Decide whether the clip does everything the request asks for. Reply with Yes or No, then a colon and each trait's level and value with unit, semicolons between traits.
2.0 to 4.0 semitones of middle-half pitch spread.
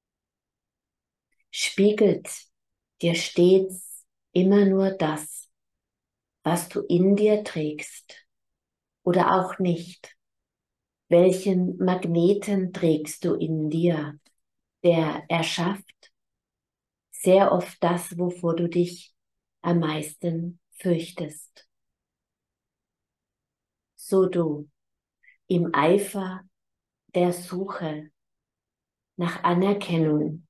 Yes: average, 2.8 semitones